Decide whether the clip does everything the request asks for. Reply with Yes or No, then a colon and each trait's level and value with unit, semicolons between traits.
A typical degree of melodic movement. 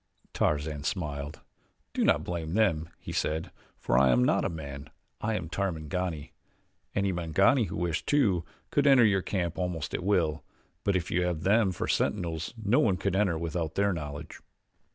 Yes: average, 4.0 semitones